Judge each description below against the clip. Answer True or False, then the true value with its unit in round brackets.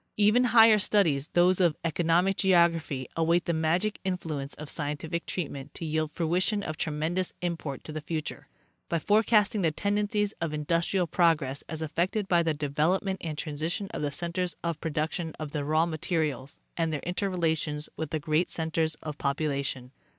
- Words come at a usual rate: True (170 wpm)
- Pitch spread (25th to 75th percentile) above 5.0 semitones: False (3.0 semitones)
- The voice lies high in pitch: False (165 Hz)